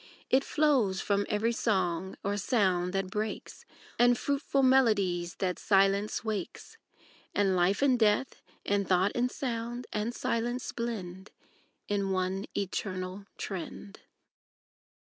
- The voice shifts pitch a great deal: No, average, 3.9 semitones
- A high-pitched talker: Yes, high, 205 Hz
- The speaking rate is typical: No, slow, 120 wpm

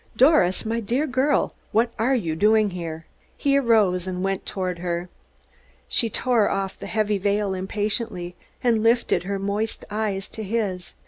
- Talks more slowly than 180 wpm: Yes, average, 155 wpm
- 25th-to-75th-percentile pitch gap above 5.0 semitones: No, average, 3.7 semitones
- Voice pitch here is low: No, high, 205 Hz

